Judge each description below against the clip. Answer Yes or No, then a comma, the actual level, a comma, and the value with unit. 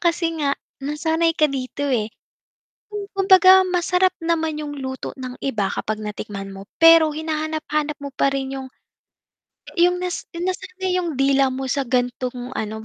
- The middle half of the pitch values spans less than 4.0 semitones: No, average, 4.6 semitones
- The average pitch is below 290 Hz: No, very high, 295 Hz